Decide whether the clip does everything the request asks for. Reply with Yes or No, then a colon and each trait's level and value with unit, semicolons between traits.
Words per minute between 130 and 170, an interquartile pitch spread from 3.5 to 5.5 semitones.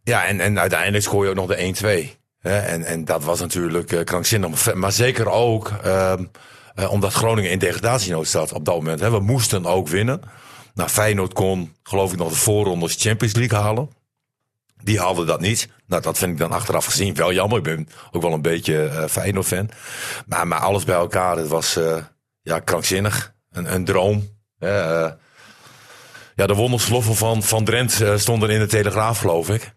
No: average, 190 wpm; average, 4.1 semitones